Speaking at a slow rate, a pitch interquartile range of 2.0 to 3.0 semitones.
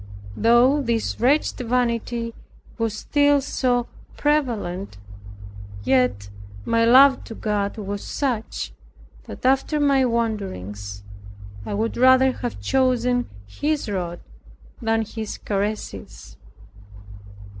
No: slow, 100 wpm; average, 4.1 semitones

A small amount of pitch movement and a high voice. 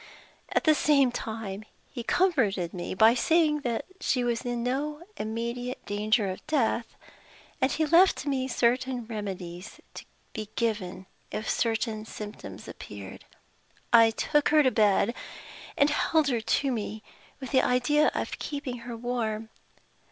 No: average, 4.1 semitones; high, 235 Hz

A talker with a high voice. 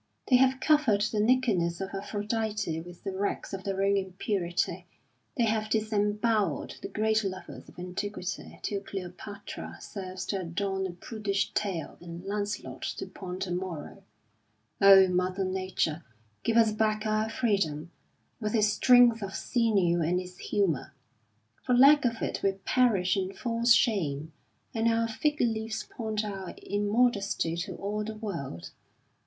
Yes: high, 205 Hz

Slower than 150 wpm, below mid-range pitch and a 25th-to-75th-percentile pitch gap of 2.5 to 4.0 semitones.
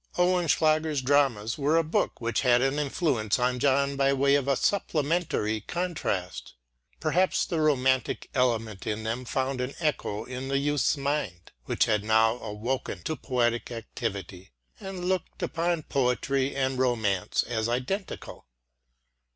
No: average, 140 wpm; low, 130 Hz; average, 4.7 semitones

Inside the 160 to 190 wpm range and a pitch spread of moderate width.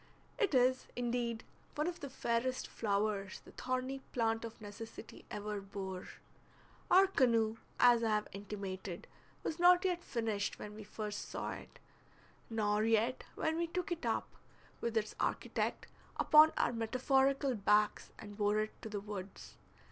No: average, 150 wpm; average, 3.7 semitones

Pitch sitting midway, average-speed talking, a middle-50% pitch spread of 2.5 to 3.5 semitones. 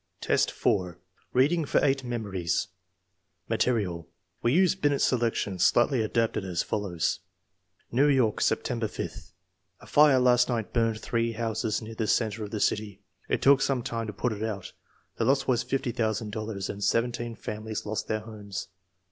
No: low, 115 Hz; average, 165 wpm; average, 2.9 semitones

